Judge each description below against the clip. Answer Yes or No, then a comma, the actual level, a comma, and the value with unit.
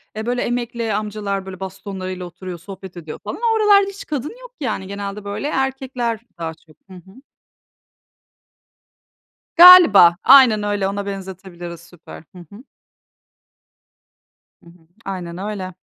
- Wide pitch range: No, average, 4.8 semitones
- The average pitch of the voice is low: No, high, 200 Hz